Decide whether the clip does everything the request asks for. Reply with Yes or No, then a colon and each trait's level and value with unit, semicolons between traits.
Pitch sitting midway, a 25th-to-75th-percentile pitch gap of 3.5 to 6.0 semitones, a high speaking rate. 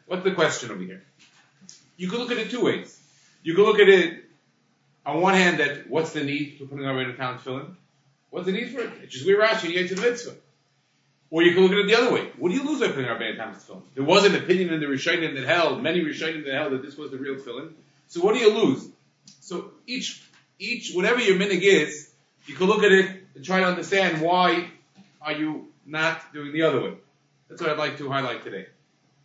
Yes: medium, 165 Hz; average, 5.1 semitones; fast, 245 wpm